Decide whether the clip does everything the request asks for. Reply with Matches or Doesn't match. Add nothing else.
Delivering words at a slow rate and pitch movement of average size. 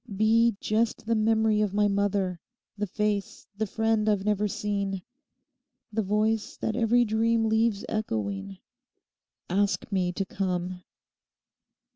Doesn't match